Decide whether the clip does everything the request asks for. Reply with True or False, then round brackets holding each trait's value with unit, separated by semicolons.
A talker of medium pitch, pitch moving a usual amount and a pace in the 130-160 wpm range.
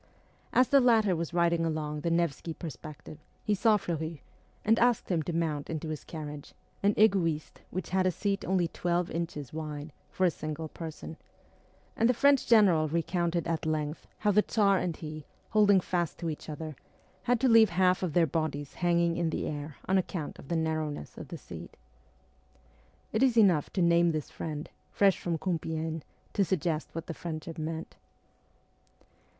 False (170 Hz; 3.2 semitones; 175 wpm)